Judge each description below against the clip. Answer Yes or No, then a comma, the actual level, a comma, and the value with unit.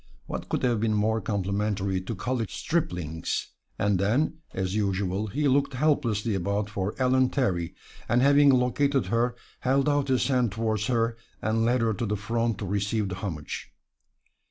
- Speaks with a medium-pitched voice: No, low, 110 Hz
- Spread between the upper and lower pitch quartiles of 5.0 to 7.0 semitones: No, average, 4.2 semitones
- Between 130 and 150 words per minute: No, average, 165 wpm